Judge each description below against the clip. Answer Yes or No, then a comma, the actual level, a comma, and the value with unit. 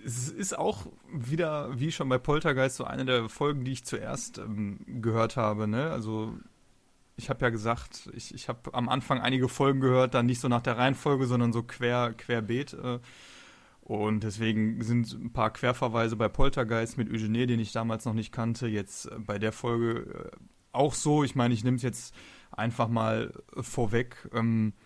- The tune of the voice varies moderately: No, narrow, 2.3 semitones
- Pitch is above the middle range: No, low, 120 Hz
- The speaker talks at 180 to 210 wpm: Yes, average, 185 wpm